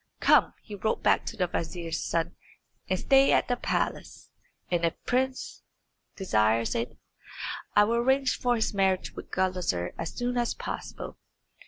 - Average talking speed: Yes, average, 160 wpm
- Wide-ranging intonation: Yes, wide, 6.5 semitones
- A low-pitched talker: No, high, 190 Hz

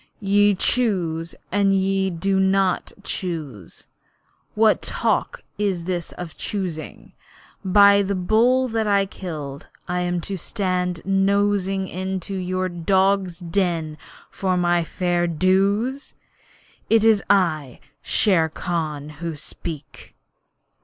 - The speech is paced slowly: Yes, slow, 110 wpm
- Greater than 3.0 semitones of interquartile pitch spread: No, average, 2.7 semitones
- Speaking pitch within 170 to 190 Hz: Yes, medium, 185 Hz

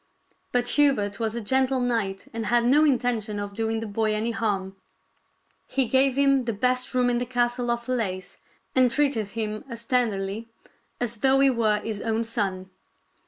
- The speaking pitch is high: Yes, high, 230 Hz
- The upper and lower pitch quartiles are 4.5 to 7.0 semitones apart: No, average, 2.9 semitones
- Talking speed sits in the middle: Yes, average, 175 wpm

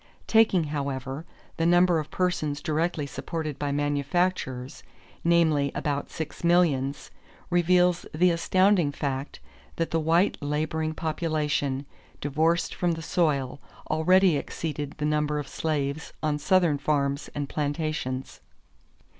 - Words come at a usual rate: No, slow, 120 wpm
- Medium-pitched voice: Yes, medium, 155 Hz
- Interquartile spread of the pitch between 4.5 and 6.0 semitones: No, average, 2.9 semitones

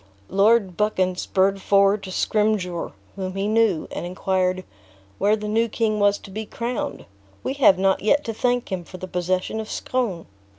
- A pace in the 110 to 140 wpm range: No, average, 175 wpm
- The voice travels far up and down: No, average, 2.8 semitones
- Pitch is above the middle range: Yes, high, 200 Hz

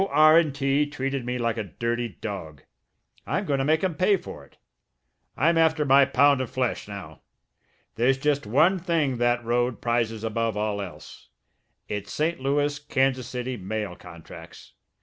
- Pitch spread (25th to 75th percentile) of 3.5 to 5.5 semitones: Yes, average, 4.5 semitones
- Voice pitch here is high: No, low, 130 Hz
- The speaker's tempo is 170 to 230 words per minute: No, average, 160 wpm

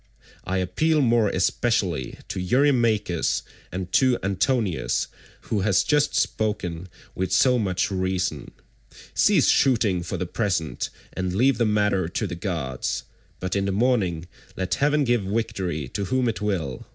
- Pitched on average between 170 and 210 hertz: No, very low, 95 Hz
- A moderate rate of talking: Yes, average, 145 wpm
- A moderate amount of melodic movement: Yes, average, 4.3 semitones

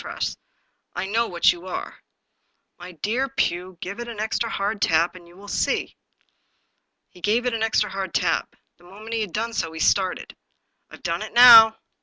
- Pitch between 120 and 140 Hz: No, high, 205 Hz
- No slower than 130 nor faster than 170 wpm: No, average, 200 wpm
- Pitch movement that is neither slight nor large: Yes, average, 4.0 semitones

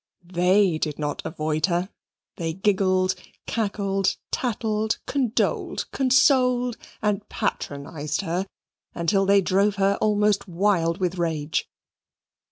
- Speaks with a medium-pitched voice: No, high, 195 Hz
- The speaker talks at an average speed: No, slow, 105 wpm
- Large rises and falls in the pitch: No, average, 3.7 semitones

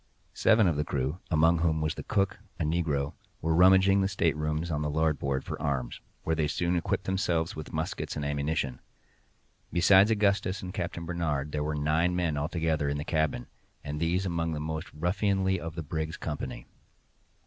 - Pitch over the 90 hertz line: No, very low, 80 Hz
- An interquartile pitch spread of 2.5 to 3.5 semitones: Yes, average, 2.8 semitones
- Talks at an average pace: Yes, average, 180 wpm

